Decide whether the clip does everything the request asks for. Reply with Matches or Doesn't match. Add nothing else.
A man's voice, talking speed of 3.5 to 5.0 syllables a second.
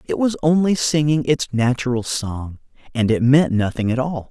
Matches